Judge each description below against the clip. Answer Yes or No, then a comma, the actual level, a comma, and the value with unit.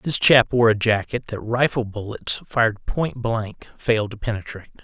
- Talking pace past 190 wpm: No, average, 175 wpm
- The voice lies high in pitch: No, low, 110 Hz